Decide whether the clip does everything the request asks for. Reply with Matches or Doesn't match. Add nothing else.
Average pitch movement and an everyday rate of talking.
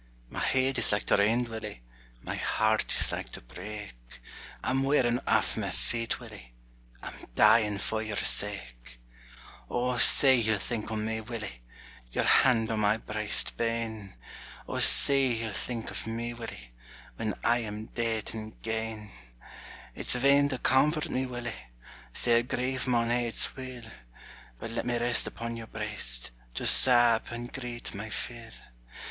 Doesn't match